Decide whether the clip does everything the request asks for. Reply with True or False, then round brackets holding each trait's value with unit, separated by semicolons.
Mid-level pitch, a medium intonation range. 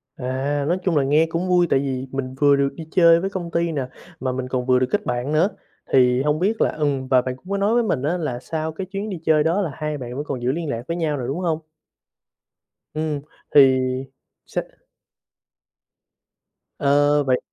True (145 Hz; 4.3 semitones)